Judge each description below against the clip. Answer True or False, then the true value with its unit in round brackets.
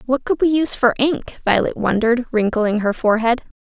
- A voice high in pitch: True (240 Hz)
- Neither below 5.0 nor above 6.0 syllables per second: True (5.6 syllables/s)